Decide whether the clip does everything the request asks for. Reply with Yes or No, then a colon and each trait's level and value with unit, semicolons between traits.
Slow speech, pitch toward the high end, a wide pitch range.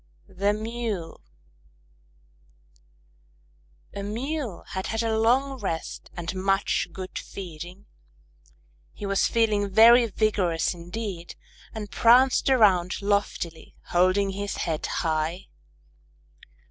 No: slow, 100 wpm; high, 200 Hz; average, 3.8 semitones